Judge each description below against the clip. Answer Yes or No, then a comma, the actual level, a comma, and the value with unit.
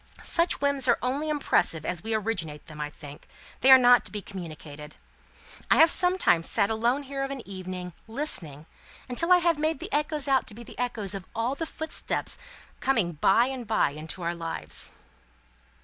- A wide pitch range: Yes, wide, 8.0 semitones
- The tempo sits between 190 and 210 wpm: Yes, average, 195 wpm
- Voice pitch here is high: Yes, high, 230 Hz